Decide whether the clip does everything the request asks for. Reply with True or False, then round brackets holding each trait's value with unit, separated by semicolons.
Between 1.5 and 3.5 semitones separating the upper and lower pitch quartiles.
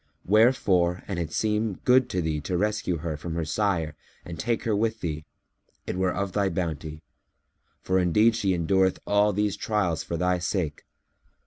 False (3.9 semitones)